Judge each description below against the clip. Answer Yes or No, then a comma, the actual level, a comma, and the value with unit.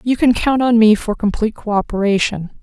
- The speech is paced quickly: No, average, 185 wpm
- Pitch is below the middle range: No, high, 220 Hz